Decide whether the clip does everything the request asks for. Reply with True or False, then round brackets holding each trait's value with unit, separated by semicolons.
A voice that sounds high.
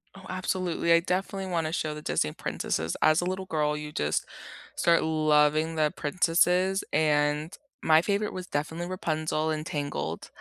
False (160 Hz)